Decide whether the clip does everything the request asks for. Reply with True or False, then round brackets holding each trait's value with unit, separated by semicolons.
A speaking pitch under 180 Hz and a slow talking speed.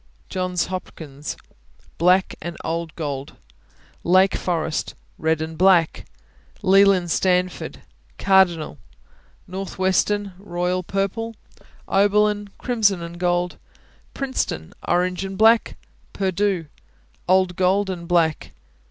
False (185 Hz; 95 wpm)